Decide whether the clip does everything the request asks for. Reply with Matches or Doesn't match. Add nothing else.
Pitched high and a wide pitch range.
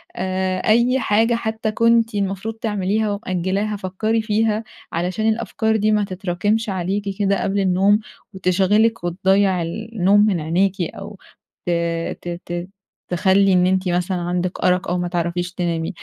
Doesn't match